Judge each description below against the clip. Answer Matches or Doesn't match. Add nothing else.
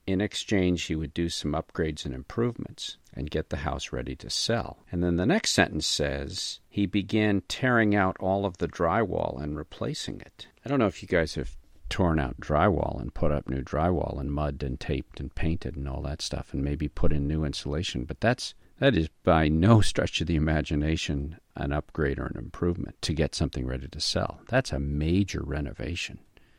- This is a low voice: Matches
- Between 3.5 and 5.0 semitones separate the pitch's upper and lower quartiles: Matches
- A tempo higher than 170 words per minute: Matches